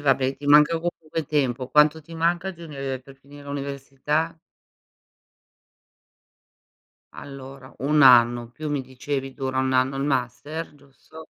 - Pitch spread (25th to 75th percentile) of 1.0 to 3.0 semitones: Yes, narrow, 2.5 semitones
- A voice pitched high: No, medium, 140 Hz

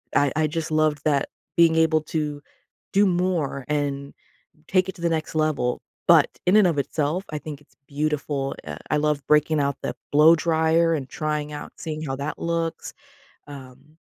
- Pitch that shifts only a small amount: Yes, narrow, 2.1 semitones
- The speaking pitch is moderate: Yes, medium, 155 Hz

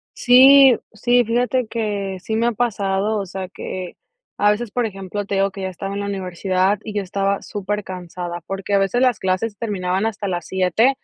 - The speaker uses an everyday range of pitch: Yes, average, 3.0 semitones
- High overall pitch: Yes, high, 200 Hz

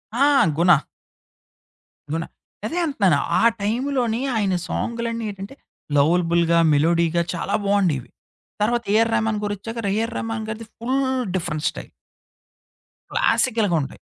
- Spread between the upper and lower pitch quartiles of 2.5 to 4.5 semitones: No, average, 5.2 semitones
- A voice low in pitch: No, high, 210 Hz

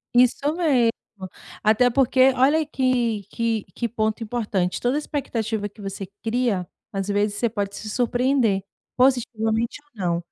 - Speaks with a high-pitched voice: Yes, high, 230 Hz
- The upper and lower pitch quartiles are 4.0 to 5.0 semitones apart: No, average, 3.6 semitones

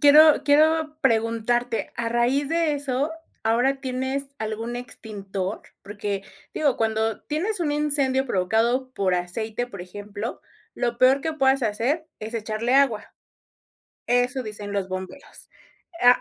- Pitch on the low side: No, high, 245 Hz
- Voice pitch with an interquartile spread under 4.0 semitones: No, average, 4.3 semitones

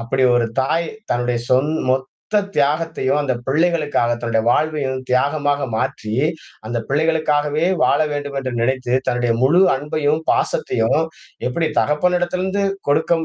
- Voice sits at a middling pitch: Yes, medium, 145 Hz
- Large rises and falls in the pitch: No, average, 3.8 semitones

